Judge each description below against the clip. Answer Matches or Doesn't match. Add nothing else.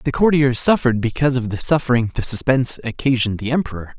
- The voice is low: Matches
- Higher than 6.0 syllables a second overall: Matches